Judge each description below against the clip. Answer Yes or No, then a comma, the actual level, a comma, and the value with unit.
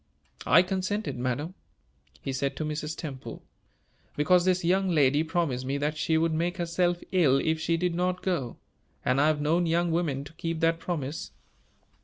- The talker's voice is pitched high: No, medium, 165 Hz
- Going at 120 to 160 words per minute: No, average, 175 wpm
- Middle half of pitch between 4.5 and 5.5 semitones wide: No, average, 3.2 semitones